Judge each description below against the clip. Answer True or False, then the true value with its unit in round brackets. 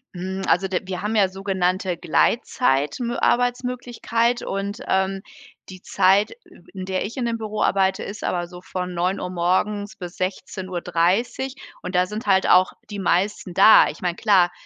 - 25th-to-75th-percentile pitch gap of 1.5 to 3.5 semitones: True (2.8 semitones)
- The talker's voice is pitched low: False (190 Hz)